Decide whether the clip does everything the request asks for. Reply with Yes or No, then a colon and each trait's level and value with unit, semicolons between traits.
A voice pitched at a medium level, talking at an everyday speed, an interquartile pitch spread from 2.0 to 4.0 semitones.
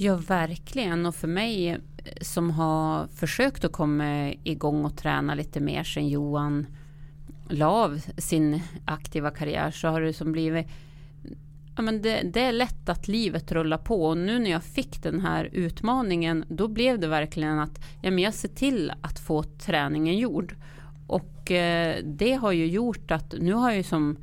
Yes: medium, 160 Hz; average, 170 wpm; average, 3.7 semitones